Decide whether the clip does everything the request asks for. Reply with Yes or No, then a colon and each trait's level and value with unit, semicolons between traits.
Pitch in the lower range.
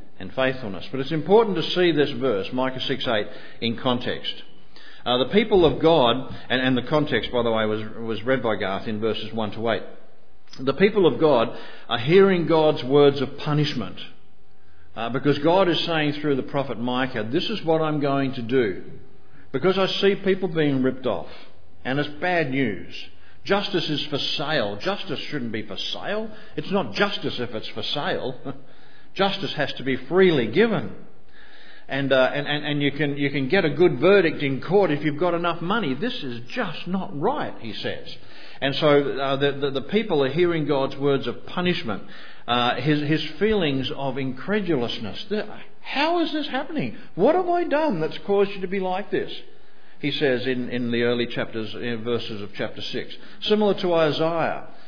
No: medium, 145 Hz